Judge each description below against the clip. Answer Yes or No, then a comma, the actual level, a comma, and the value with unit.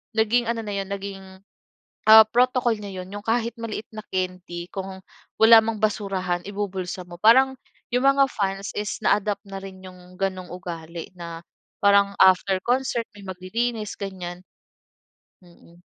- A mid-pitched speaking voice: No, high, 195 Hz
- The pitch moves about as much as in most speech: Yes, average, 3.1 semitones